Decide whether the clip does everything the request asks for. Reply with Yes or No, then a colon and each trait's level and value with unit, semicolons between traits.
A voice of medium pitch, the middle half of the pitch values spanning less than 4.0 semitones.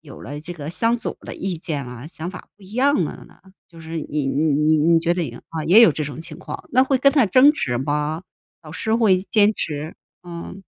No: medium, 165 Hz; average, 5.3 semitones